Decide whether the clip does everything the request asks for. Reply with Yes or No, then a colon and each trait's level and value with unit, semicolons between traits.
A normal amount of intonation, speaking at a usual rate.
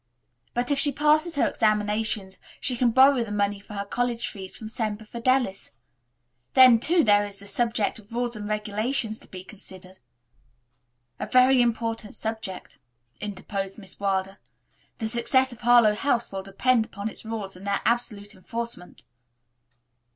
Yes: average, 3.2 semitones; average, 155 wpm